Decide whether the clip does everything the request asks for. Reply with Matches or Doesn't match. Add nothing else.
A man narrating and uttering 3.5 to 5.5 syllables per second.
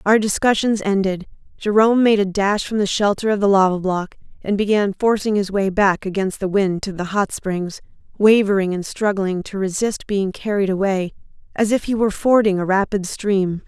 Doesn't match